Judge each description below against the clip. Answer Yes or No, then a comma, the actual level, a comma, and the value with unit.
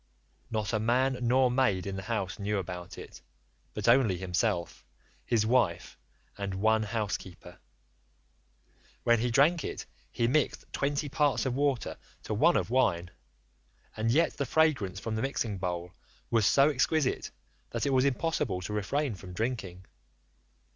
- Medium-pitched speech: No, low, 115 Hz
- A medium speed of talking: Yes, average, 150 wpm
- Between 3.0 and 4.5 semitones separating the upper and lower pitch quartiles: No, wide, 5.5 semitones